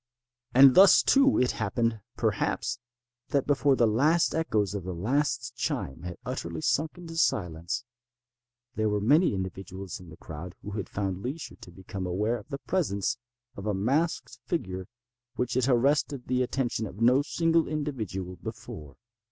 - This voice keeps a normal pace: Yes, average, 160 wpm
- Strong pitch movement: Yes, wide, 7.0 semitones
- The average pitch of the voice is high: No, low, 115 Hz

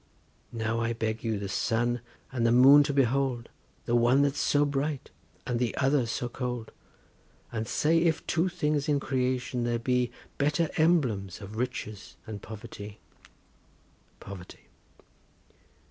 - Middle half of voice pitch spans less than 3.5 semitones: No, average, 3.8 semitones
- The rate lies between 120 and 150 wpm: Yes, average, 140 wpm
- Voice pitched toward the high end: No, low, 125 Hz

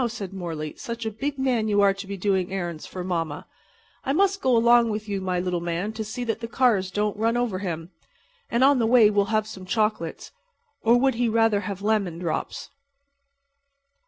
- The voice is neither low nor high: No, high, 210 Hz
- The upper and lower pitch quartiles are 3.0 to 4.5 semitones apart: Yes, average, 3.8 semitones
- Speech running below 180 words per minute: No, average, 195 wpm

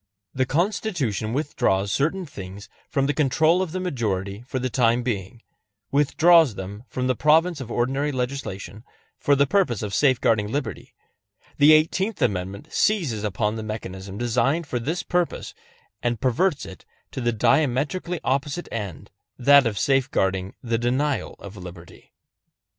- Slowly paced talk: No, average, 145 wpm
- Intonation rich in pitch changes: Yes, wide, 6.0 semitones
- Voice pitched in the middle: No, low, 130 Hz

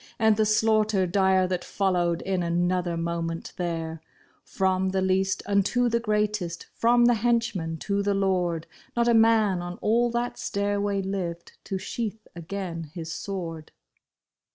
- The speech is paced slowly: No, average, 150 wpm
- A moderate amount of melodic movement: Yes, average, 3.6 semitones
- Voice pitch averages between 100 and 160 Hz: No, high, 190 Hz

